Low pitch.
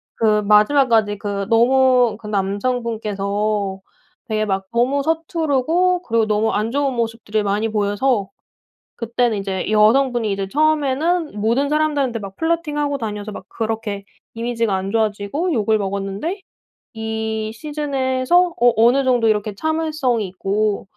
No: high, 225 Hz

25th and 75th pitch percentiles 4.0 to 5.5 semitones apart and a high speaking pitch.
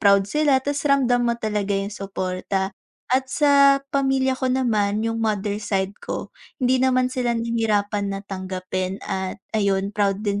Yes: average, 4.5 semitones; high, 215 Hz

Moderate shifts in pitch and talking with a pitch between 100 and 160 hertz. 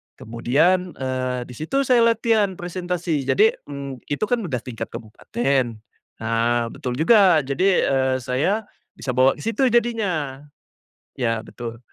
No: wide, 7.5 semitones; medium, 140 Hz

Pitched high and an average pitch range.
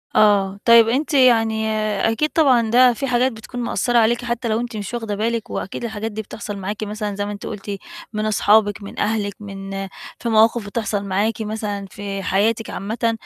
No: high, 220 Hz; narrow, 2.2 semitones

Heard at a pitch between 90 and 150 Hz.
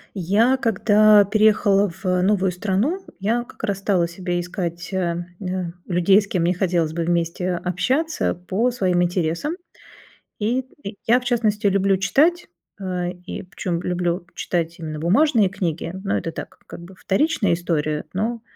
No: high, 190 Hz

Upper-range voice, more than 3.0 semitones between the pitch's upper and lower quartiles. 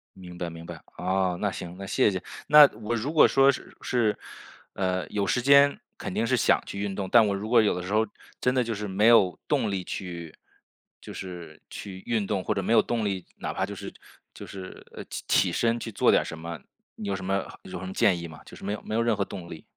No: low, 100 Hz; average, 3.8 semitones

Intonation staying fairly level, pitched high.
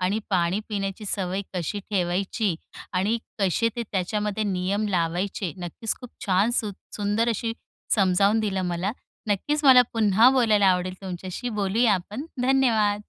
No: average, 3.1 semitones; high, 200 Hz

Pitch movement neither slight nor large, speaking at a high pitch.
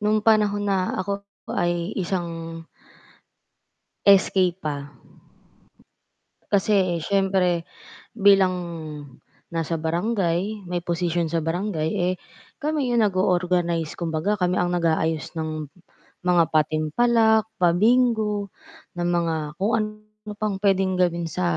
No: average, 3.5 semitones; medium, 180 Hz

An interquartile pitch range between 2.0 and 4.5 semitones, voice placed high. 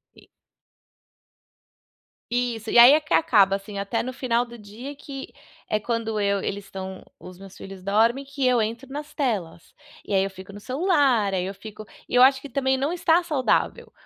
No: average, 5.1 semitones; high, 230 Hz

